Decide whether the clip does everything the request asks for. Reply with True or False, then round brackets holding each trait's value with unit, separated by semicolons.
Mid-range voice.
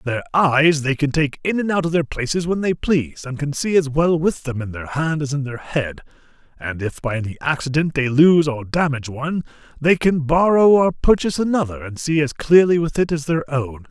True (150 Hz)